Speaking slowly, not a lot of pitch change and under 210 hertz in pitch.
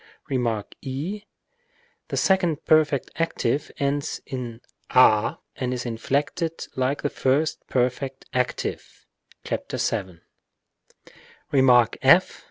No: slow, 100 wpm; average, 3.1 semitones; low, 135 Hz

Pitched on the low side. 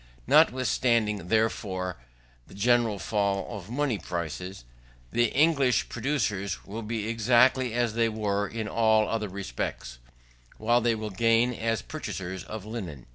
Yes: low, 110 Hz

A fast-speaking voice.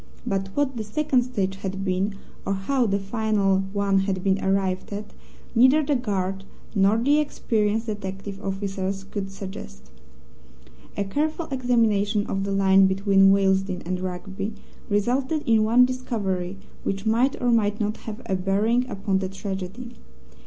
No: average, 150 wpm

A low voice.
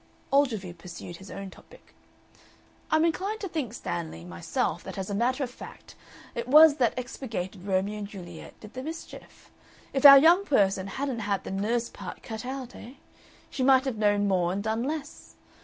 No: high, 225 Hz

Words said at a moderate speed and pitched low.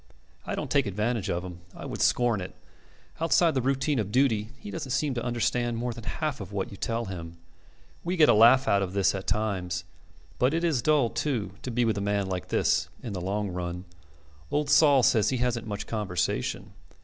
No: fast, 210 wpm; low, 115 Hz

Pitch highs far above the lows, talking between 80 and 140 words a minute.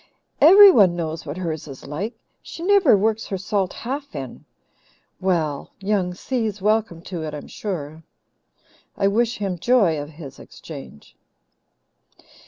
Yes: wide, 5.8 semitones; slow, 135 wpm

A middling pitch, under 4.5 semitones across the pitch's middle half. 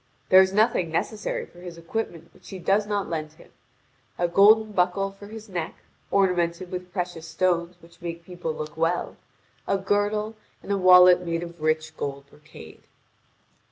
Yes: medium, 180 Hz; average, 2.8 semitones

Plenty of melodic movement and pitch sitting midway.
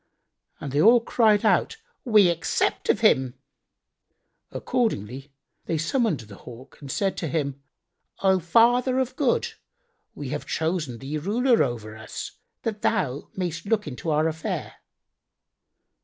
Yes: wide, 8.4 semitones; medium, 170 Hz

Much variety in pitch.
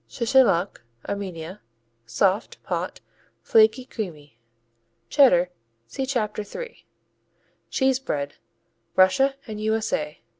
Yes: wide, 6.7 semitones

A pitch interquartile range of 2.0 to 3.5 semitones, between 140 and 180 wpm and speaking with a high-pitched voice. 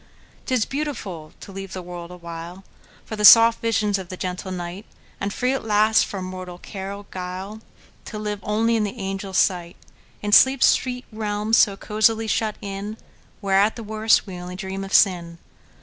Yes: average, 2.8 semitones; average, 170 wpm; high, 200 Hz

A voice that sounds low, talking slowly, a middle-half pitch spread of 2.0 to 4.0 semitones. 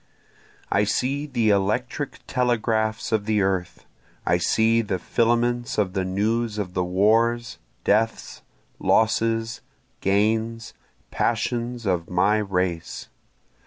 Yes: low, 110 Hz; slow, 110 wpm; average, 3.0 semitones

